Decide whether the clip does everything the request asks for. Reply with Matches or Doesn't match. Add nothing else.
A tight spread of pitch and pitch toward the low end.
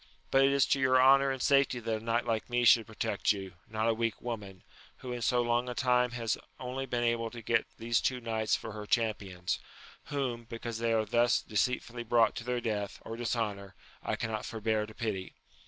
Matches